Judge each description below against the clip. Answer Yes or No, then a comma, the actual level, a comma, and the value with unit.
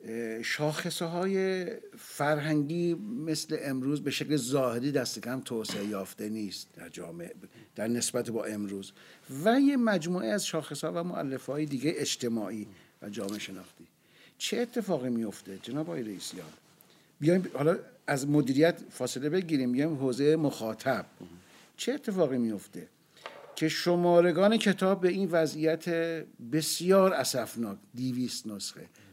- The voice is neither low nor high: Yes, medium, 150 Hz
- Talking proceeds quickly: No, average, 130 wpm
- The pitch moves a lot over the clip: Yes, wide, 6.5 semitones